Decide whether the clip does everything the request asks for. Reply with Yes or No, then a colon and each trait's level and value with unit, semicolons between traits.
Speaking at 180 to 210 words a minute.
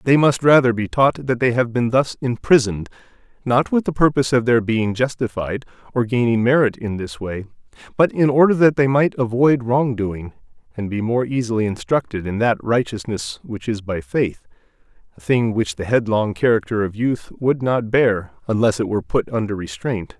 Yes: average, 185 wpm